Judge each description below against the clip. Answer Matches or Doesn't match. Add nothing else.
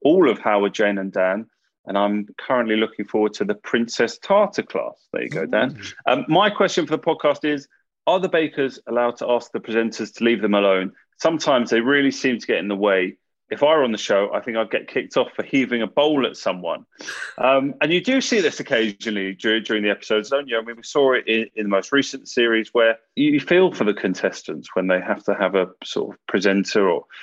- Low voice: Matches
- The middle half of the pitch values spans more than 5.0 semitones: Matches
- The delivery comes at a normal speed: Doesn't match